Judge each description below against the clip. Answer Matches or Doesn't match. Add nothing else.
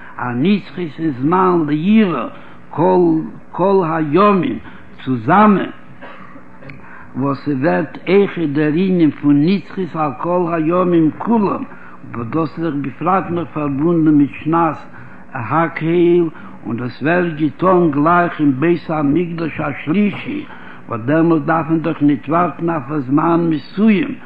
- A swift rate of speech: Doesn't match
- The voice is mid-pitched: Matches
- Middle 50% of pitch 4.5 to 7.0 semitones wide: Doesn't match